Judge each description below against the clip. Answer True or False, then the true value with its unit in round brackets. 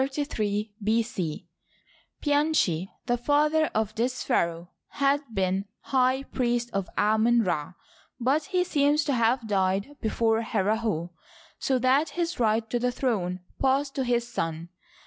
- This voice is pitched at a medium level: False (235 Hz)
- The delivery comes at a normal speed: False (130 wpm)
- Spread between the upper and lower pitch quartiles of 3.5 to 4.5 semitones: False (5.1 semitones)